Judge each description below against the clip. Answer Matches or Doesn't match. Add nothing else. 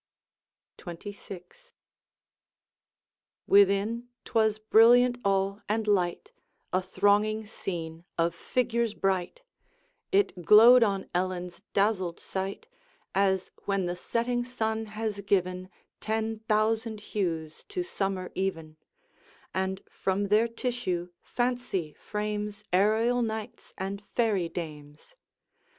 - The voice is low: Doesn't match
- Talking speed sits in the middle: Doesn't match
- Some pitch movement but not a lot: Matches